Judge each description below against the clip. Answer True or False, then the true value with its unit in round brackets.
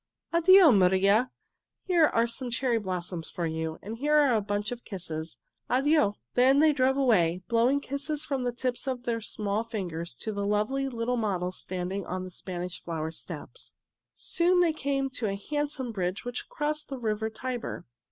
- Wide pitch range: True (6.1 semitones)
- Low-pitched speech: False (230 Hz)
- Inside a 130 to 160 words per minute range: False (175 wpm)